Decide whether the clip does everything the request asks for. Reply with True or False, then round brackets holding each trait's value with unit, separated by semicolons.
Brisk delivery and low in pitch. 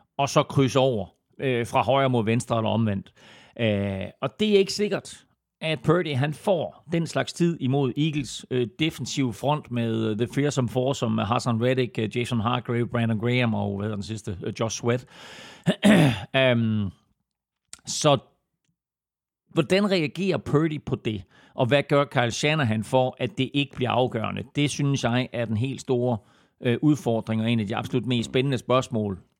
False (175 wpm; 125 Hz)